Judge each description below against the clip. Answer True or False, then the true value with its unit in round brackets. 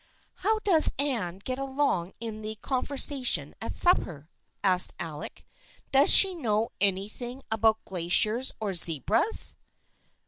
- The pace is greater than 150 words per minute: False (140 wpm)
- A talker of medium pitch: False (220 Hz)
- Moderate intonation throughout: False (6.4 semitones)